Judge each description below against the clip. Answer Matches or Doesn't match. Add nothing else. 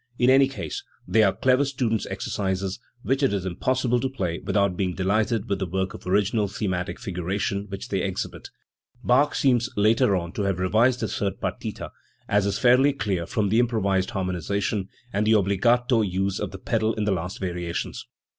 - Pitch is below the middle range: Matches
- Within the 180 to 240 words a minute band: Matches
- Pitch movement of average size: Matches